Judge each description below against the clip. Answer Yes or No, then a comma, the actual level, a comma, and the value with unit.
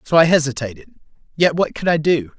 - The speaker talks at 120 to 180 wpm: No, average, 200 wpm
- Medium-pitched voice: Yes, medium, 155 Hz